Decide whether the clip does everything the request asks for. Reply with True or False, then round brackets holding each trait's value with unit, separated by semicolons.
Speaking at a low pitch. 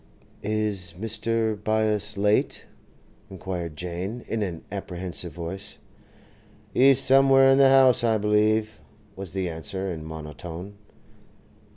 True (100 Hz)